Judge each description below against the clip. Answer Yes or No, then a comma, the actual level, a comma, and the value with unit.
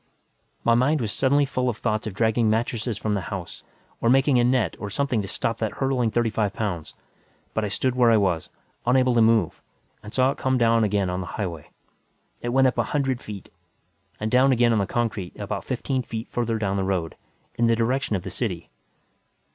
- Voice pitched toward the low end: Yes, low, 115 Hz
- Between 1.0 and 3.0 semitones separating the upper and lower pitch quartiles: No, average, 3.5 semitones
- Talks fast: Yes, fast, 210 wpm